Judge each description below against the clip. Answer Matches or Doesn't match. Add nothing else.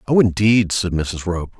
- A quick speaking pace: Doesn't match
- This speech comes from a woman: Doesn't match